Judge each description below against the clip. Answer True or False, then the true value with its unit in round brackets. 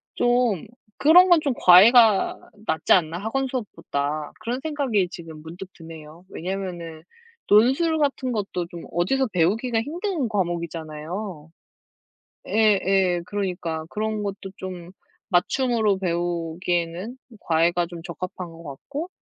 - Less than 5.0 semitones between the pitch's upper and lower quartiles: False (5.5 semitones)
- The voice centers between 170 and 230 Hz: True (190 Hz)